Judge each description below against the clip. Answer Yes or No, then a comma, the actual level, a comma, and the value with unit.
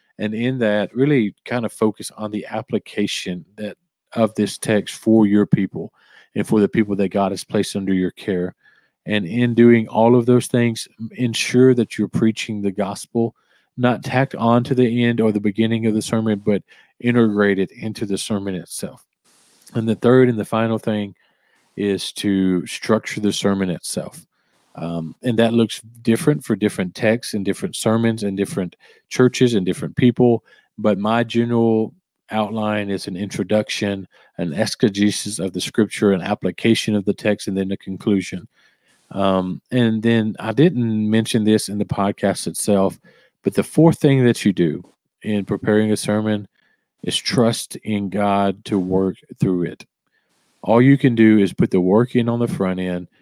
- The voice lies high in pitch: No, low, 105 Hz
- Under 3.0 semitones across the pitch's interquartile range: Yes, narrow, 2.6 semitones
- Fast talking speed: No, average, 175 wpm